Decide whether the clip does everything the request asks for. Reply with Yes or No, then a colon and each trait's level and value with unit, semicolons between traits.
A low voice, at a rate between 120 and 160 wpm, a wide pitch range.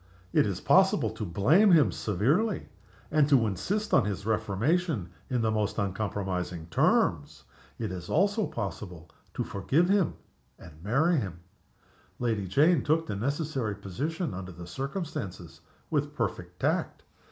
Yes: low, 110 Hz; average, 140 wpm; wide, 8.6 semitones